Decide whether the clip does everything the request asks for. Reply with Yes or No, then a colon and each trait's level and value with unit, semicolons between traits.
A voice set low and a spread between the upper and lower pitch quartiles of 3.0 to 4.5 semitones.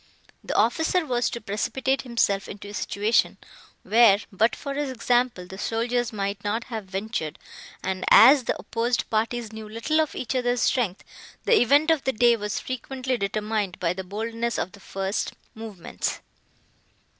No: high, 225 Hz; average, 3.5 semitones